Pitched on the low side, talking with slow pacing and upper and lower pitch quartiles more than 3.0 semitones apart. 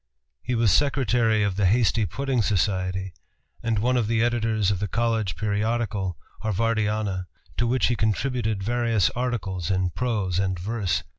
No: low, 110 Hz; average, 150 wpm; average, 3.5 semitones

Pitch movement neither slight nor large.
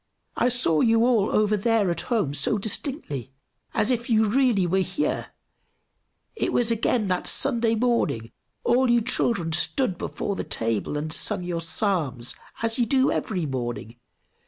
No: wide, 6.3 semitones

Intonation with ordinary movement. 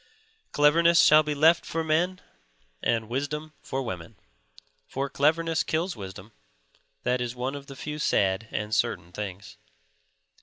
No: wide, 5.8 semitones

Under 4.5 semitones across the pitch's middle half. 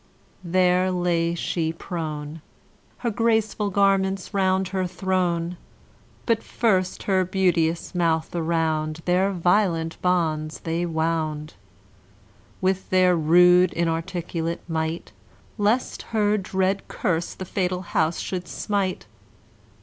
Yes: narrow, 2.4 semitones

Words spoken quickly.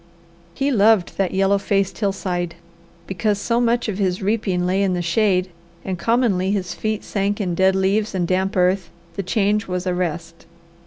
No: average, 175 wpm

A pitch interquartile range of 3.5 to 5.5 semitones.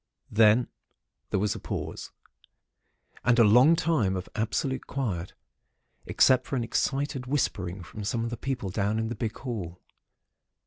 Yes: average, 4.2 semitones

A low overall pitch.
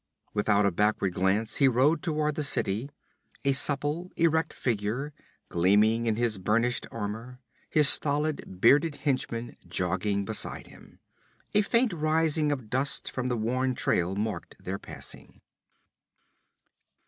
Yes: low, 125 Hz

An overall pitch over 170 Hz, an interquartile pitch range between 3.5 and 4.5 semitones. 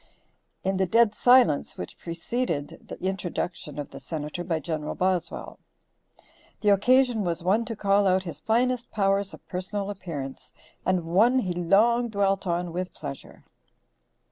Yes: high, 190 Hz; average, 4.0 semitones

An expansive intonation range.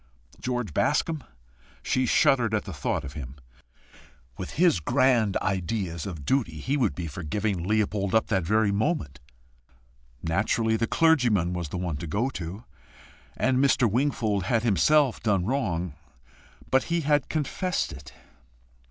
Yes: wide, 6.7 semitones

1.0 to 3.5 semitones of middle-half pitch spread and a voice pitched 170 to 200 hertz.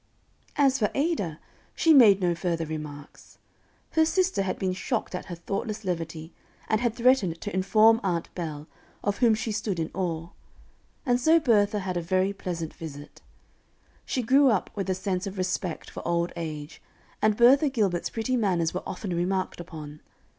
No: average, 4.9 semitones; high, 190 Hz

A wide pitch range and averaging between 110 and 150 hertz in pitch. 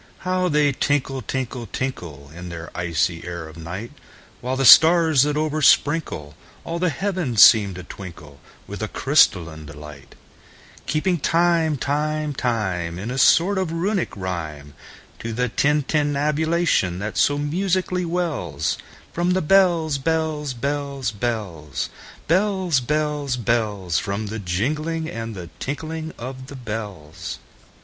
Yes: wide, 8.8 semitones; low, 135 Hz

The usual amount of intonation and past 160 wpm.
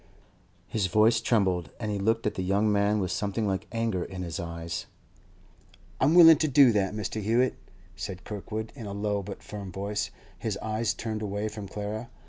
No: narrow, 2.3 semitones; average, 185 wpm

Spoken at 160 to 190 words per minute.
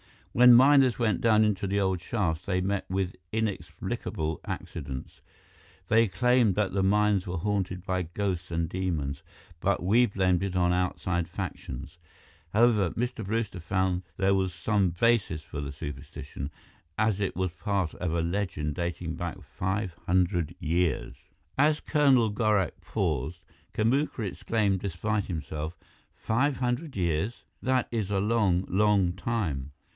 No: average, 140 wpm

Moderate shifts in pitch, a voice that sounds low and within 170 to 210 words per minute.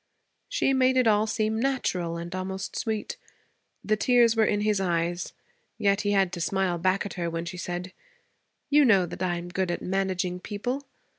No: average, 3.7 semitones; high, 195 Hz; average, 190 wpm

